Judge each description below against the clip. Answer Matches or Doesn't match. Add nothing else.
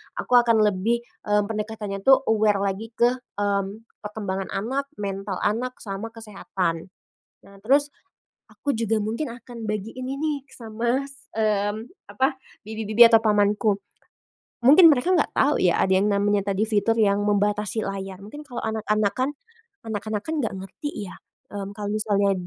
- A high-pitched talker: Matches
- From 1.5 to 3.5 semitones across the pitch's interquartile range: Matches